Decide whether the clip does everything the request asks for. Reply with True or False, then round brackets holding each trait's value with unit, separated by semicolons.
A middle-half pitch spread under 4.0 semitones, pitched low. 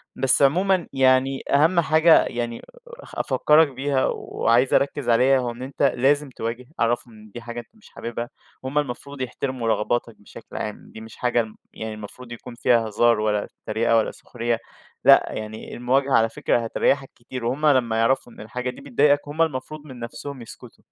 True (3.1 semitones; 125 Hz)